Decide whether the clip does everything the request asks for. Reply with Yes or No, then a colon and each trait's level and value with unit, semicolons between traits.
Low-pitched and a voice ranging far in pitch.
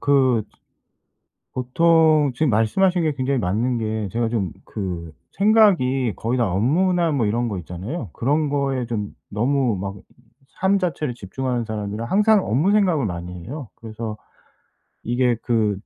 Yes: low, 125 Hz; wide, 6.0 semitones